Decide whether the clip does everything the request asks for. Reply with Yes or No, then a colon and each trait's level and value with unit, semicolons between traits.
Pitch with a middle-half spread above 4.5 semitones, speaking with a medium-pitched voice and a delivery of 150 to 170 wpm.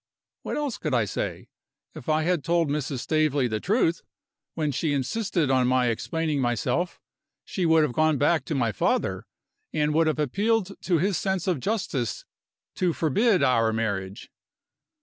Yes: average, 5.2 semitones; medium, 155 Hz; average, 165 wpm